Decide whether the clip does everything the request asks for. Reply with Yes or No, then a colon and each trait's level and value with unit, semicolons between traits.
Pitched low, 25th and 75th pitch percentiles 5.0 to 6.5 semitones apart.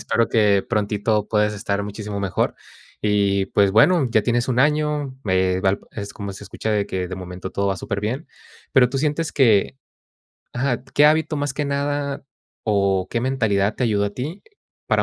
Yes: low, 105 Hz; average, 5.3 semitones